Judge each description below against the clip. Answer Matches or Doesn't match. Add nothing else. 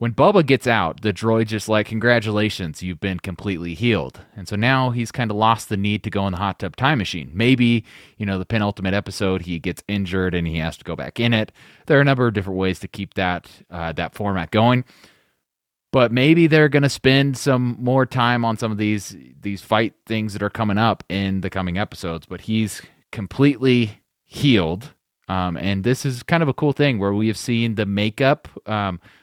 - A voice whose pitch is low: Matches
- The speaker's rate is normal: Doesn't match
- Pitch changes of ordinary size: Matches